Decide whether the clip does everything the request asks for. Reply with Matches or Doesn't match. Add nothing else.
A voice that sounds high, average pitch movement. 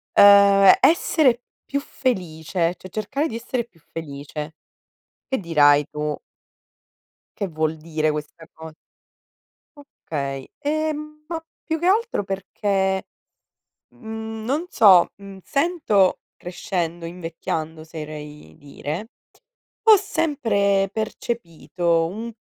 Doesn't match